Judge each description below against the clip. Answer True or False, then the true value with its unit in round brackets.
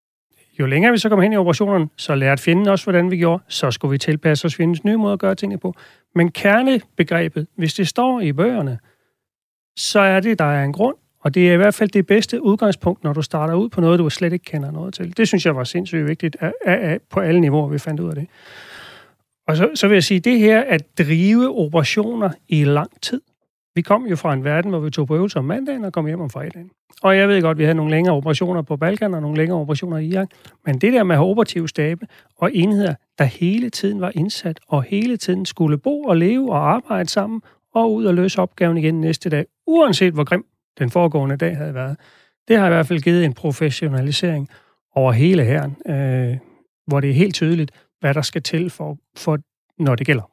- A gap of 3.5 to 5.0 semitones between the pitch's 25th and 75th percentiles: True (4.2 semitones)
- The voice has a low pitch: False (170 Hz)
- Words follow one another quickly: True (235 wpm)